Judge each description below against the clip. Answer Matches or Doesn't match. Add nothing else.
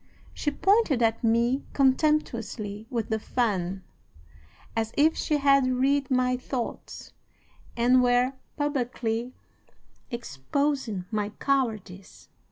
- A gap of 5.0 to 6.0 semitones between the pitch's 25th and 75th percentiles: Doesn't match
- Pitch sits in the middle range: Doesn't match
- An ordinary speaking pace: Doesn't match